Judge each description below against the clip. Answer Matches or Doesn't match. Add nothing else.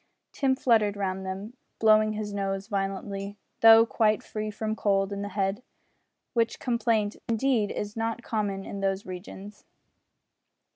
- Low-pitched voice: Doesn't match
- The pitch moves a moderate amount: Doesn't match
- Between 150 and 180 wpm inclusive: Doesn't match